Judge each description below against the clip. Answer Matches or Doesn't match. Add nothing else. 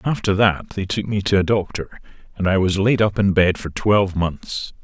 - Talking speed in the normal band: Doesn't match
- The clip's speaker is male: Matches